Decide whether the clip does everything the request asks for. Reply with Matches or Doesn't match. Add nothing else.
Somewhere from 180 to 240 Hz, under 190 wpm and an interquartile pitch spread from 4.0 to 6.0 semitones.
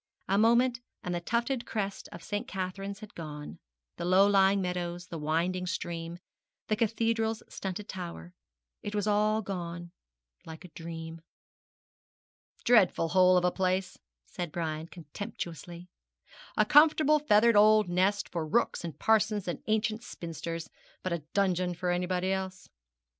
Doesn't match